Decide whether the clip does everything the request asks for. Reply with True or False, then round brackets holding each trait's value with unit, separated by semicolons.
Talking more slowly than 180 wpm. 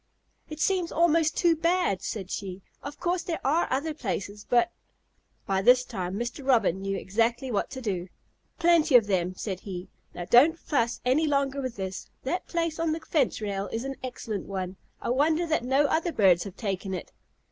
False (190 wpm)